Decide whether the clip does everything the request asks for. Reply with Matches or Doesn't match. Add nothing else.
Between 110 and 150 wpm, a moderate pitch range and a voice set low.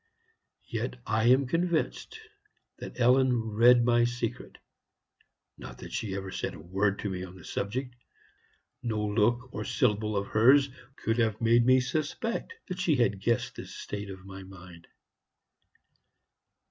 Matches